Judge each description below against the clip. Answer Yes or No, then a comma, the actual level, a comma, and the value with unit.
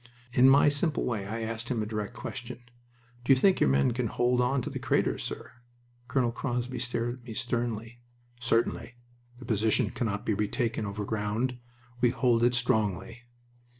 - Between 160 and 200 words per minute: Yes, average, 170 wpm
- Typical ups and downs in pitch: No, narrow, 2.2 semitones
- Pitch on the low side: Yes, low, 120 Hz